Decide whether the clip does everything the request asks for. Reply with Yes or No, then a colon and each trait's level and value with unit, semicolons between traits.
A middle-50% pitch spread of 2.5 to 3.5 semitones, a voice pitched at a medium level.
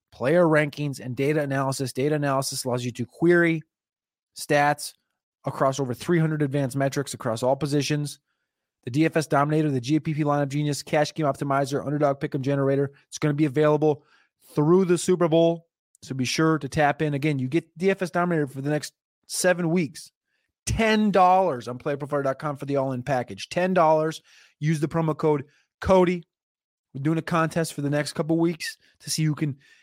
Yes: average, 2.8 semitones; medium, 150 Hz